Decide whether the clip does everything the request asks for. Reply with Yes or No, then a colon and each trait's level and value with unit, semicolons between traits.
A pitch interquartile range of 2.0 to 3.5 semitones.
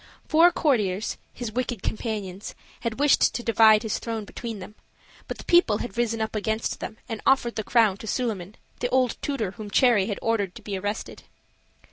Yes: average, 2.7 semitones